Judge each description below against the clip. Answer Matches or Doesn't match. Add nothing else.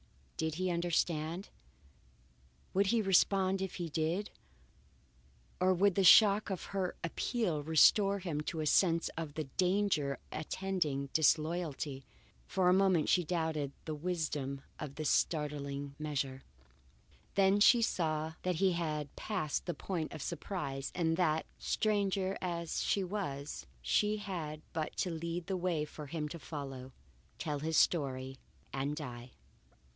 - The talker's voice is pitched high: Doesn't match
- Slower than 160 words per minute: Matches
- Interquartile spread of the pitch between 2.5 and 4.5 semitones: Matches